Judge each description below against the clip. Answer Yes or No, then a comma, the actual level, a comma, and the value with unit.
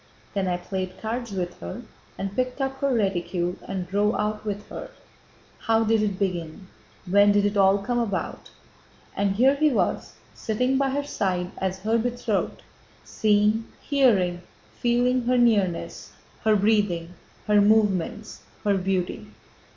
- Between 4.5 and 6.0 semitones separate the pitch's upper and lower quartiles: No, average, 3.6 semitones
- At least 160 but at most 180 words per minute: No, average, 145 wpm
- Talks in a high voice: Yes, high, 205 Hz